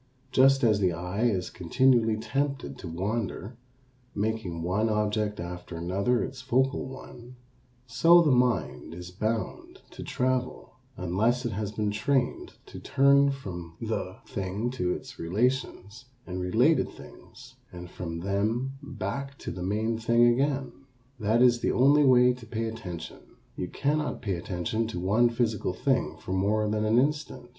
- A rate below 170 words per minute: Yes, average, 150 wpm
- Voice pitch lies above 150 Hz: No, low, 110 Hz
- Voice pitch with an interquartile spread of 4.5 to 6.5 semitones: Yes, average, 5.3 semitones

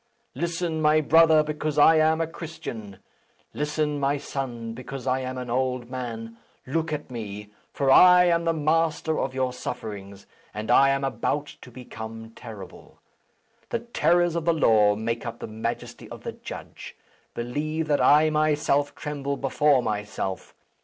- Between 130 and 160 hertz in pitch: Yes, medium, 140 Hz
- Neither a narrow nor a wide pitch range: Yes, average, 5.0 semitones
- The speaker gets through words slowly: No, average, 155 wpm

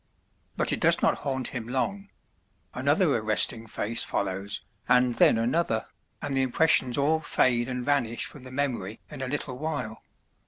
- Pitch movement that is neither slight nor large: Yes, average, 3.5 semitones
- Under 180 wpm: Yes, average, 160 wpm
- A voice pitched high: No, low, 125 Hz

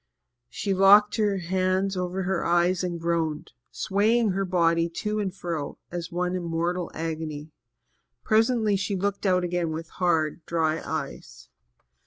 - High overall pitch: No, medium, 180 Hz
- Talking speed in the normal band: Yes, average, 145 wpm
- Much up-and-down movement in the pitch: No, average, 2.7 semitones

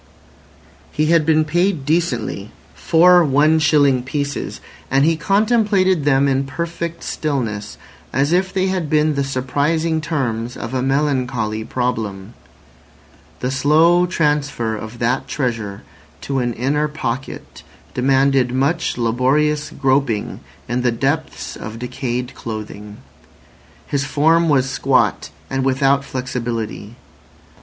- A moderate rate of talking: No, slow, 115 wpm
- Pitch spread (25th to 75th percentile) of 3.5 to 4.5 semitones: Yes, average, 4.0 semitones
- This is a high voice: No, low, 135 Hz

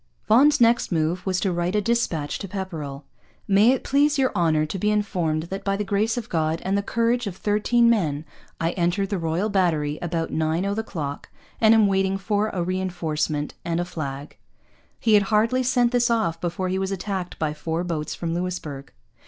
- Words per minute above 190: Yes, average, 200 wpm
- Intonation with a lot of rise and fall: No, average, 4.4 semitones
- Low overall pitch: No, high, 190 Hz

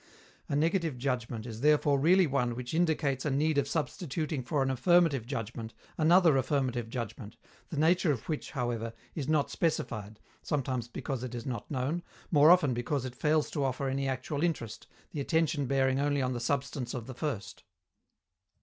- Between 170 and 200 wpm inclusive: Yes, average, 175 wpm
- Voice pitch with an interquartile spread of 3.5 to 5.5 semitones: Yes, average, 3.8 semitones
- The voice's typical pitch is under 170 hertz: Yes, low, 135 Hz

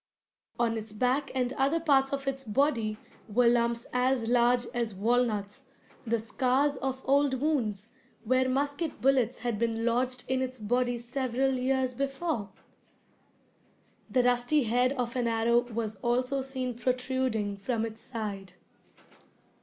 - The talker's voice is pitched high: Yes, very high, 250 Hz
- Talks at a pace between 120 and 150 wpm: Yes, average, 140 wpm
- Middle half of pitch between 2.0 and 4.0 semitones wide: Yes, narrow, 2.5 semitones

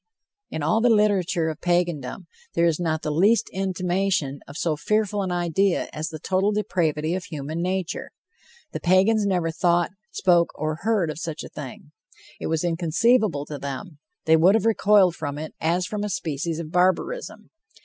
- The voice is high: No, medium, 175 Hz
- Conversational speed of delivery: Yes, average, 175 wpm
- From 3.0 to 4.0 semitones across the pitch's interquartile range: Yes, average, 3.6 semitones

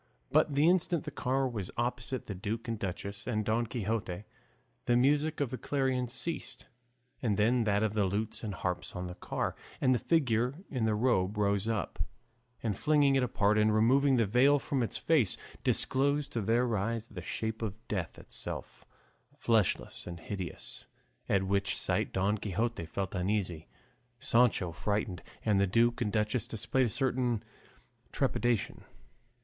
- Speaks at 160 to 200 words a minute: Yes, average, 165 wpm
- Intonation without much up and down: No, average, 4.0 semitones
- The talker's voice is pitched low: Yes, low, 110 Hz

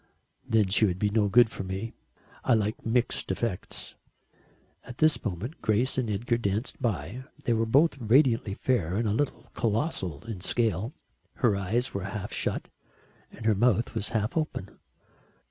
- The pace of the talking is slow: No, average, 160 wpm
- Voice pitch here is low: Yes, low, 110 Hz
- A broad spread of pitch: No, average, 3.3 semitones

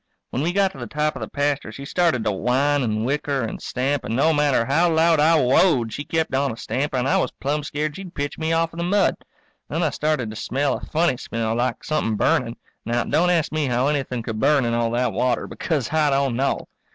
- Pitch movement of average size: Yes, average, 4.2 semitones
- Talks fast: Yes, fast, 245 wpm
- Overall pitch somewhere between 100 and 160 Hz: Yes, medium, 140 Hz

